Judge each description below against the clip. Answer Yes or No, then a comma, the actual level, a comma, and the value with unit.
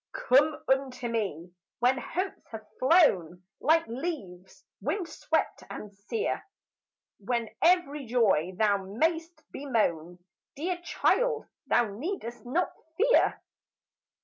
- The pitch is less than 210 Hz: No, very high, 250 Hz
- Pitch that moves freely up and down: Yes, wide, 8.3 semitones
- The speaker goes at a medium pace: No, slow, 105 wpm